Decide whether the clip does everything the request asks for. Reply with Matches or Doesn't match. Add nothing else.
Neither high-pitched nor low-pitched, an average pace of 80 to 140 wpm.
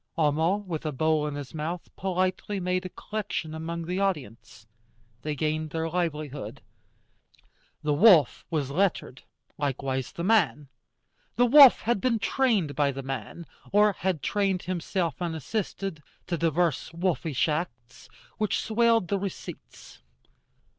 Matches